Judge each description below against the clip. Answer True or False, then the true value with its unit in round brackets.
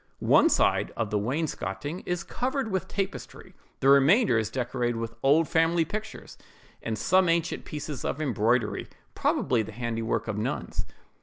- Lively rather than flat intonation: True (6.8 semitones)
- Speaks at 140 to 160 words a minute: True (150 wpm)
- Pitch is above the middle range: False (135 Hz)